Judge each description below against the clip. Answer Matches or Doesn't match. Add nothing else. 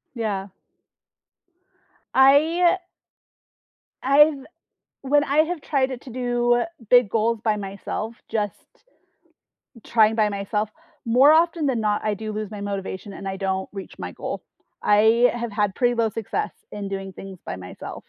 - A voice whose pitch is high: Matches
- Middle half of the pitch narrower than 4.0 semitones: Doesn't match